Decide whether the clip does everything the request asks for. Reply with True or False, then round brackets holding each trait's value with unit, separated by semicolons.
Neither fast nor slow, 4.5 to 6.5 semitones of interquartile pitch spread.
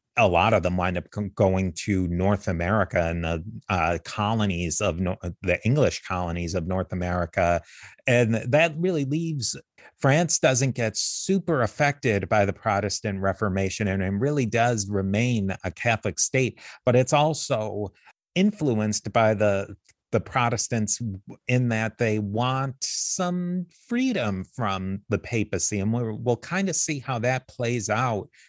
True (145 wpm; 4.9 semitones)